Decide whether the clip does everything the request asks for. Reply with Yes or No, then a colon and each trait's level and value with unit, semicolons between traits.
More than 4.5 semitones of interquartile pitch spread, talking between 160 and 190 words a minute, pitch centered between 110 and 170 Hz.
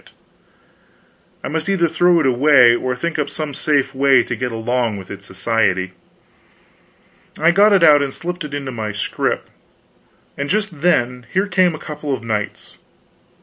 Yes: wide, 5.6 semitones; average, 170 wpm; medium, 140 Hz